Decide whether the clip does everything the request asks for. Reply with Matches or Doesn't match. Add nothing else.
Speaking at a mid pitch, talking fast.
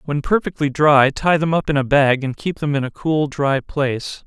Matches